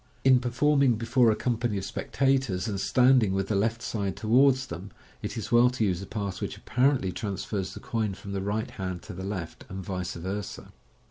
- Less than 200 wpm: No, fast, 205 wpm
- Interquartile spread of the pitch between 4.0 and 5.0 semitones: Yes, average, 4.3 semitones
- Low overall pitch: Yes, low, 105 Hz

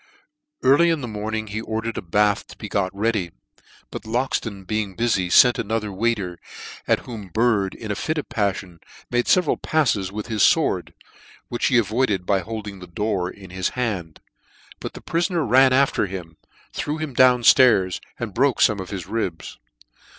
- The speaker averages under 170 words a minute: No, average, 175 wpm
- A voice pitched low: Yes, low, 110 Hz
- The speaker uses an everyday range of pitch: Yes, average, 4.0 semitones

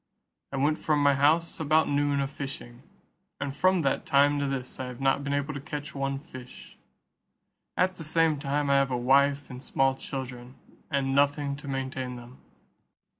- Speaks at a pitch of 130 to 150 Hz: Yes, medium, 140 Hz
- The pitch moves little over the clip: Yes, narrow, 1.4 semitones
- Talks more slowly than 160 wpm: No, average, 180 wpm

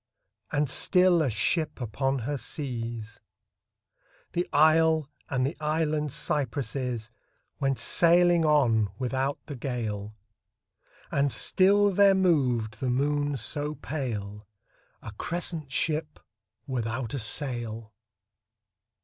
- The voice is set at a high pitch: No, medium, 140 Hz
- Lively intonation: No, average, 4.6 semitones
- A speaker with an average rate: No, slow, 105 wpm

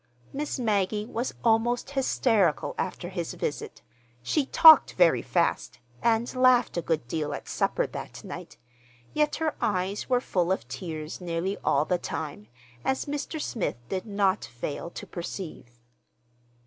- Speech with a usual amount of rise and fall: No, wide, 6.5 semitones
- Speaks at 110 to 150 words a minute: Yes, average, 145 wpm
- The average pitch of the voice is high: Yes, high, 195 Hz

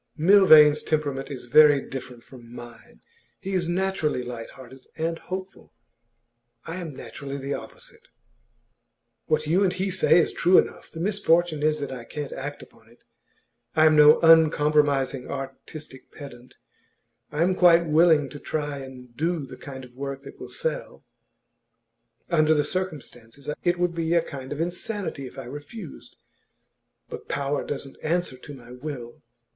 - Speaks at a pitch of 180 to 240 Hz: No, medium, 150 Hz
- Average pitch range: Yes, average, 4.1 semitones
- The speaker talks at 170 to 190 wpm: No, average, 155 wpm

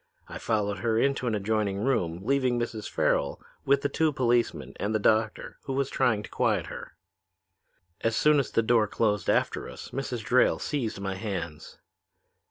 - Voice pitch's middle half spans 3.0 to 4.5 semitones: Yes, average, 3.8 semitones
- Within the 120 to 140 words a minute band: No, average, 175 wpm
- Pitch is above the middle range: No, low, 110 Hz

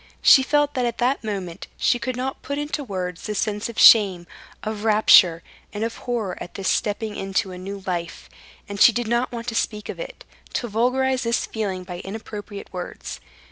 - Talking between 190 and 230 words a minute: Yes, average, 195 wpm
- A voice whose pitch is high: Yes, high, 215 Hz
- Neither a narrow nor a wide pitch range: Yes, average, 3.9 semitones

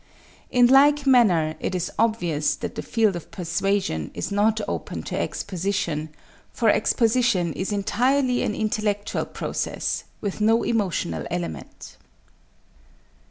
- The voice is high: Yes, high, 205 Hz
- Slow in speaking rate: Yes, slow, 120 wpm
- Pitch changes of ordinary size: Yes, average, 4.8 semitones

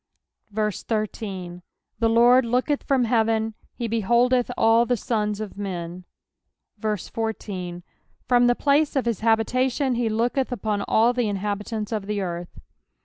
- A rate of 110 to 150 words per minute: Yes, average, 140 wpm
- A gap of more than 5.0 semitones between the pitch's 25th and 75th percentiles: No, average, 2.9 semitones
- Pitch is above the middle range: Yes, high, 225 Hz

